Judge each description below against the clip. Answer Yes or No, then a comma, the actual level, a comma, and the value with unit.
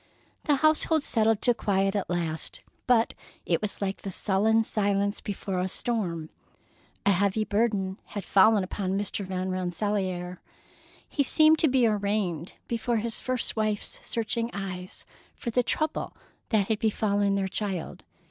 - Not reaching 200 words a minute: Yes, average, 150 wpm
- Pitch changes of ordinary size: Yes, average, 3.0 semitones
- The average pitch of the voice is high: Yes, high, 205 Hz